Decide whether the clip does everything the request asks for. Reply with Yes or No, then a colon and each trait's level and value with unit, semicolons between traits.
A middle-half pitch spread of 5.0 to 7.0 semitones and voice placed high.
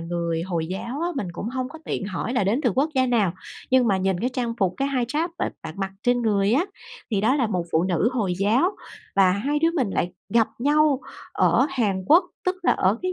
Yes: wide, 5.6 semitones; high, 230 Hz